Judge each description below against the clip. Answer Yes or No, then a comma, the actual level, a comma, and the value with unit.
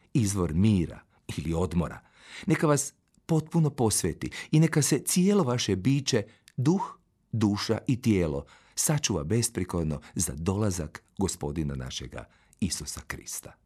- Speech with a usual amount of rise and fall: No, wide, 8.6 semitones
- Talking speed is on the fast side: No, average, 115 wpm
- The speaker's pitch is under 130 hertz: Yes, low, 110 Hz